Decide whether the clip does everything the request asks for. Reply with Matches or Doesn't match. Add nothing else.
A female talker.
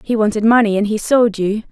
Matches